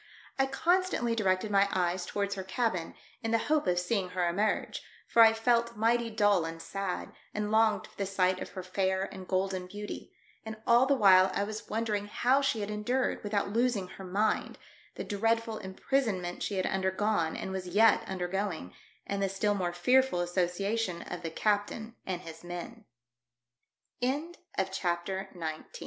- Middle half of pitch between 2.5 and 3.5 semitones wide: Yes, average, 3.2 semitones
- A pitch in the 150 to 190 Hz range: No, high, 205 Hz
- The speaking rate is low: No, average, 150 wpm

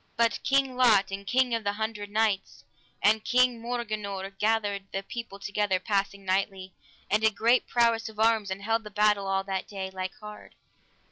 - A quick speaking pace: No, average, 180 wpm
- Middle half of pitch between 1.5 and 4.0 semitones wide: Yes, narrow, 2.6 semitones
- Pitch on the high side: Yes, high, 210 Hz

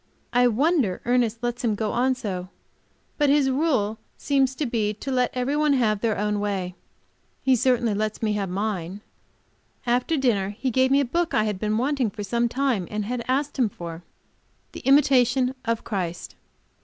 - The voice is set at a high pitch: Yes, high, 235 Hz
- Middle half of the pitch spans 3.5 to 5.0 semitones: Yes, average, 4.0 semitones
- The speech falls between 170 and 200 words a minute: Yes, average, 180 wpm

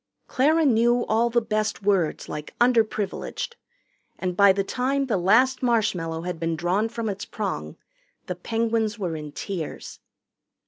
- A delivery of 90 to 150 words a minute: Yes, average, 145 wpm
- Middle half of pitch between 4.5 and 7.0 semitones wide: Yes, average, 4.8 semitones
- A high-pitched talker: Yes, high, 215 Hz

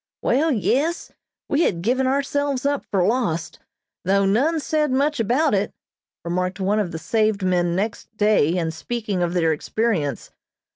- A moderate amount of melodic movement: No, wide, 6.8 semitones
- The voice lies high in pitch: Yes, high, 215 Hz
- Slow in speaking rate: No, average, 155 wpm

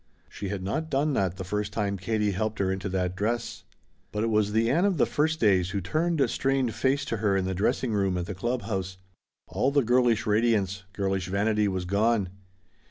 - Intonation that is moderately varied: Yes, average, 3.7 semitones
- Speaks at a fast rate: Yes, fast, 210 wpm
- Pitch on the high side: No, low, 105 Hz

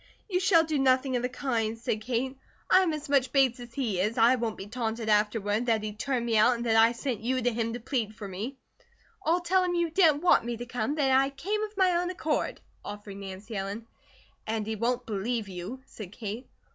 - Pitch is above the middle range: Yes, high, 240 Hz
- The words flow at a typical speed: No, fast, 230 wpm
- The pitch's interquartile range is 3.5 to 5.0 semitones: Yes, average, 4.2 semitones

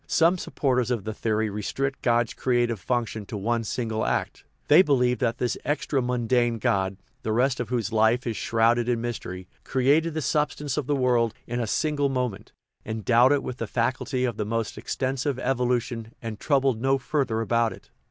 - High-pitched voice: No, low, 120 Hz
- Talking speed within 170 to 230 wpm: Yes, average, 180 wpm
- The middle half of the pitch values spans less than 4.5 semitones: Yes, average, 2.7 semitones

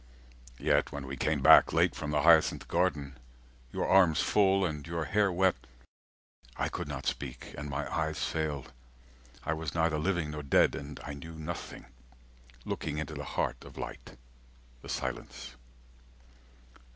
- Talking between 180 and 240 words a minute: No, average, 155 wpm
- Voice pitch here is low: Yes, very low, 75 Hz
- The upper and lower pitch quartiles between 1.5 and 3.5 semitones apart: Yes, narrow, 2.5 semitones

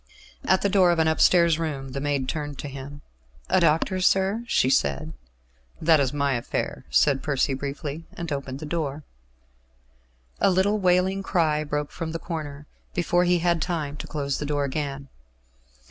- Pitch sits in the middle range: Yes, medium, 155 Hz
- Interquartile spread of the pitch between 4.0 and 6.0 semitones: No, average, 3.6 semitones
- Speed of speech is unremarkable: Yes, average, 170 wpm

